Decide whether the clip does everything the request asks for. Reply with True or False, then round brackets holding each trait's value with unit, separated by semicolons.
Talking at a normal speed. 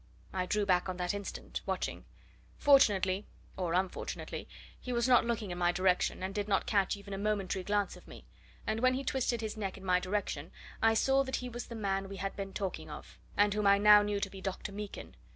False (225 wpm)